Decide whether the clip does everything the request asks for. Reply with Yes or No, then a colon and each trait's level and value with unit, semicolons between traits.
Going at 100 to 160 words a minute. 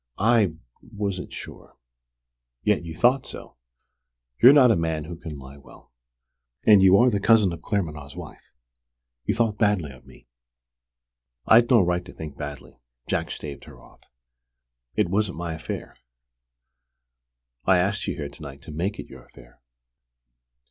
Yes: average, 155 wpm